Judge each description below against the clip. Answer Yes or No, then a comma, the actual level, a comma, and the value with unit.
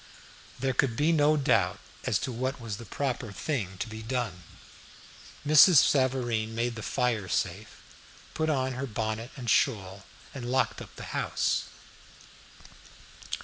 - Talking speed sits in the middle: Yes, average, 145 wpm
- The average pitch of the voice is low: Yes, low, 120 Hz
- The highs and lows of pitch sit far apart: No, average, 3.5 semitones